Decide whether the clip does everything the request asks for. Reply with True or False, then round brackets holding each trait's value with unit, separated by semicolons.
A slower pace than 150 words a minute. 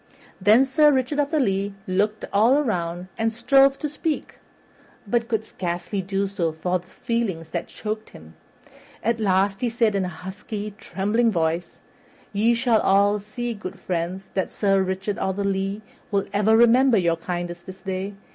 False (170 wpm)